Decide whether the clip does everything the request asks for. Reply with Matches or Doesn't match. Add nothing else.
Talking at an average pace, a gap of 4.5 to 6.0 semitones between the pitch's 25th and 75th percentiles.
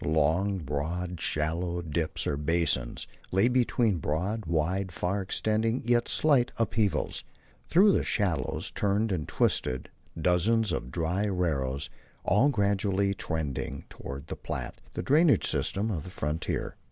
Doesn't match